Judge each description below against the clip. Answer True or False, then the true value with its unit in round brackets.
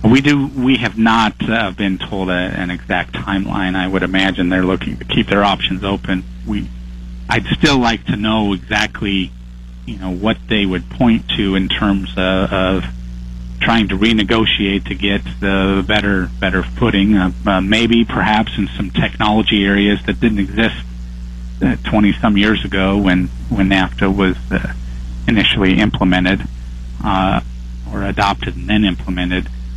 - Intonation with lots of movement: True (8.2 semitones)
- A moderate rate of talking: True (155 wpm)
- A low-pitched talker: True (95 Hz)